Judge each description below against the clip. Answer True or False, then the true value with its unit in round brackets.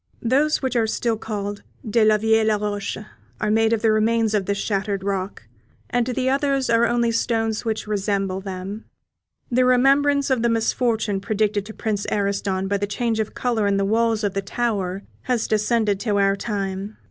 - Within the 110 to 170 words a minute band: False (180 wpm)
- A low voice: False (215 Hz)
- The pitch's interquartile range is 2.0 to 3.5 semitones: True (2.6 semitones)